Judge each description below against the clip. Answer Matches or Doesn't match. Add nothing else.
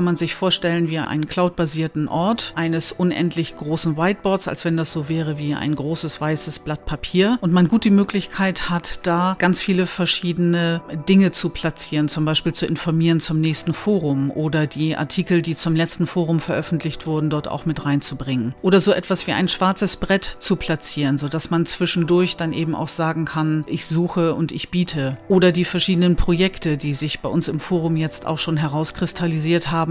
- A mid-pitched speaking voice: Matches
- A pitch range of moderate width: Doesn't match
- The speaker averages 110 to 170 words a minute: Doesn't match